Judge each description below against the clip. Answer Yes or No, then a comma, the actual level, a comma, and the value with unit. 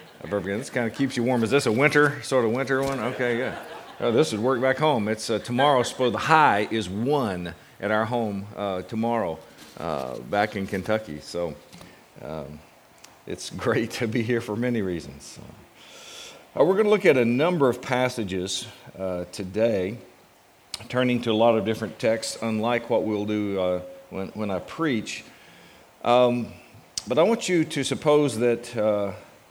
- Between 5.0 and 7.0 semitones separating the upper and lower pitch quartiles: No, average, 3.9 semitones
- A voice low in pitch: Yes, low, 115 Hz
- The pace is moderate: Yes, average, 180 wpm